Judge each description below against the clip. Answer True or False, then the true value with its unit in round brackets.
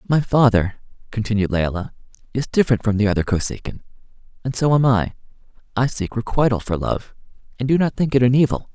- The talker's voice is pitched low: True (120 Hz)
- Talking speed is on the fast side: False (180 wpm)